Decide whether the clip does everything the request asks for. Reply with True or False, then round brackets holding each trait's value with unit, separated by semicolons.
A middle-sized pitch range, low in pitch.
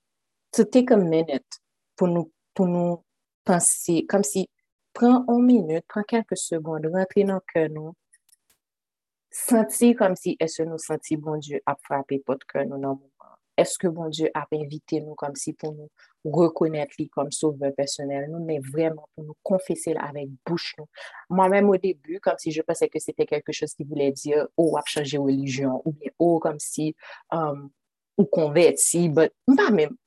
False (3.7 semitones; 160 Hz)